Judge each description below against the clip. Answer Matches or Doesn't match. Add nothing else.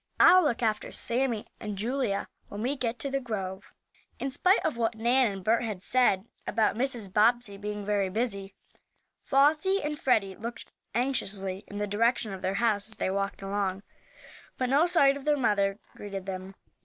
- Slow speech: Doesn't match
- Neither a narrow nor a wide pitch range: Matches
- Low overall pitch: Doesn't match